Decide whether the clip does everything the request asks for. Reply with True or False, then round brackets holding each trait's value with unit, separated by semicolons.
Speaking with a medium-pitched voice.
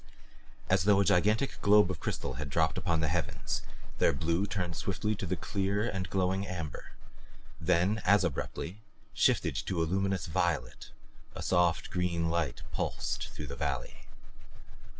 False (90 Hz)